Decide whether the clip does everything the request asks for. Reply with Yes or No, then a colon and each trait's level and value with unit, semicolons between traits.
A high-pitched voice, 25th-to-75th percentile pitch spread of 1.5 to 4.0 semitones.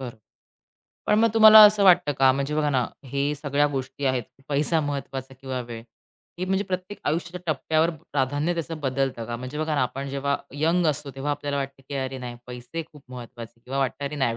No: medium, 140 Hz; average, 3.1 semitones